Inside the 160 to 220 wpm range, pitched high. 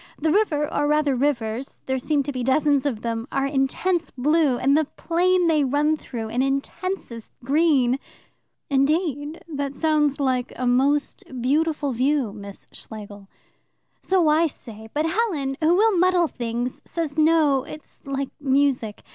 No: average, 150 wpm; very high, 285 Hz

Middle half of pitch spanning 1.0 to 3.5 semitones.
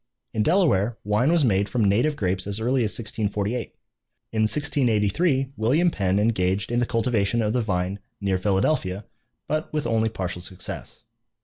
No: average, 4.2 semitones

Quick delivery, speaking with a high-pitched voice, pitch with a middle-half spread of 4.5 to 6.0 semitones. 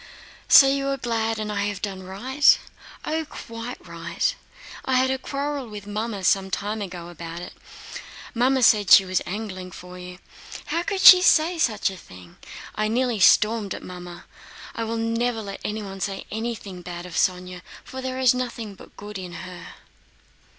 No: average, 175 wpm; high, 210 Hz; average, 5.0 semitones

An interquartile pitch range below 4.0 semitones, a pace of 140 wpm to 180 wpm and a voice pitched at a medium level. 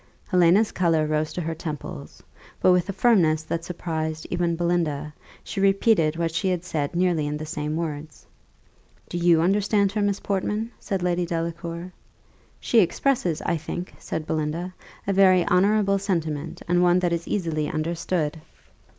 Yes: average, 2.8 semitones; average, 160 wpm; medium, 170 Hz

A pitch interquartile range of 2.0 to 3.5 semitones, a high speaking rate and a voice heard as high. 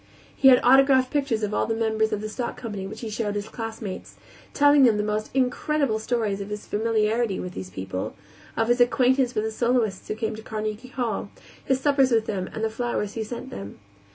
Yes: average, 2.9 semitones; fast, 210 wpm; high, 225 Hz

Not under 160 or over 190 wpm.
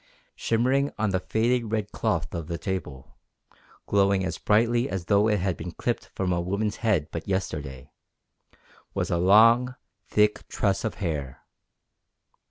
No: average, 150 wpm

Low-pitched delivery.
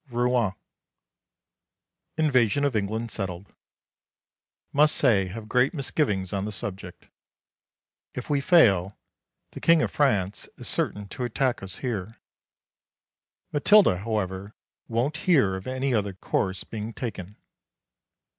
Yes: low, 110 Hz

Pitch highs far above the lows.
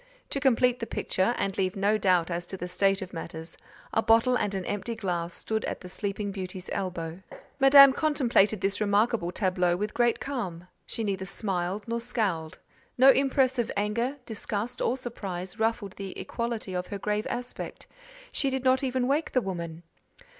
No: average, 4.6 semitones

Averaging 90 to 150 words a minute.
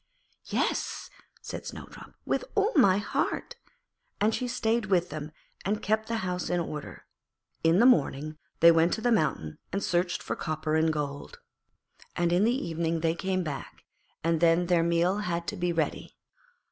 No: average, 170 wpm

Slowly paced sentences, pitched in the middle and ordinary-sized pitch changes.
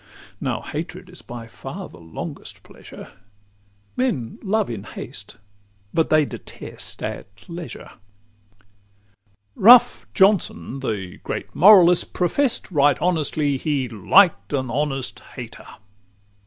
No: slow, 115 wpm; medium, 150 Hz; wide, 7.0 semitones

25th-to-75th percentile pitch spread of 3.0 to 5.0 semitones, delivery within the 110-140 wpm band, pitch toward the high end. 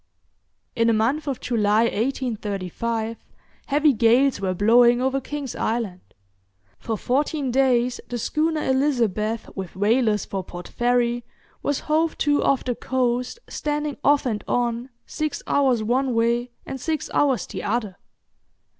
Yes: average, 3.4 semitones; slow, 135 wpm; high, 245 Hz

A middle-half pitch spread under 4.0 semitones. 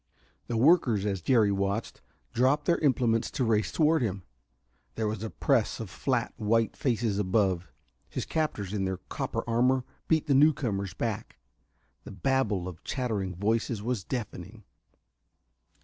No: average, 4.5 semitones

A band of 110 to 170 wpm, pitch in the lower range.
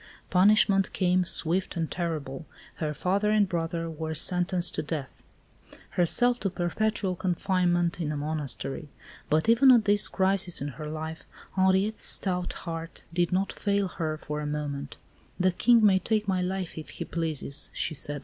No: average, 160 wpm; medium, 175 Hz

